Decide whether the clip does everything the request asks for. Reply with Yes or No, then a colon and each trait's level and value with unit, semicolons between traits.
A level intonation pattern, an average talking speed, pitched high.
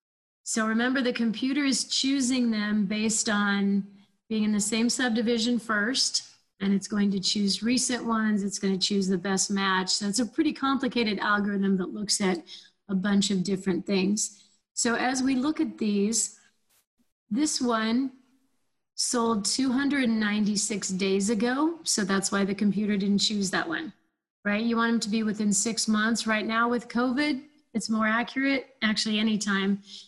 No: average, 3.3 semitones; average, 165 wpm; high, 215 Hz